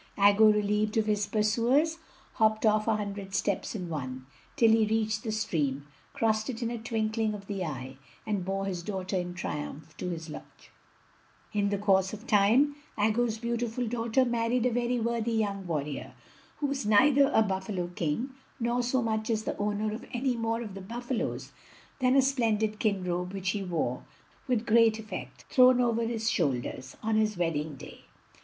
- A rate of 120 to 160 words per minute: No, average, 180 wpm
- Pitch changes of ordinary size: Yes, average, 3.3 semitones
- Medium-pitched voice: No, high, 215 Hz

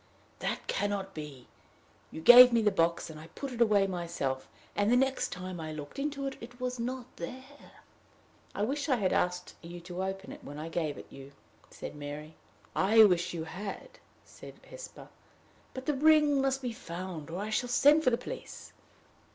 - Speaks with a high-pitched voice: Yes, high, 200 Hz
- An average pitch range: No, wide, 7.2 semitones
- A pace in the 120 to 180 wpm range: No, average, 190 wpm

